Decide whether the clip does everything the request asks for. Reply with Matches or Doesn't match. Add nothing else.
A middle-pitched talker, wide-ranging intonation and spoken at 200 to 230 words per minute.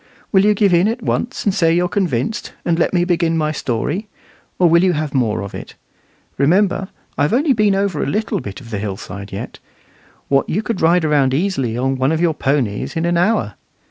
Matches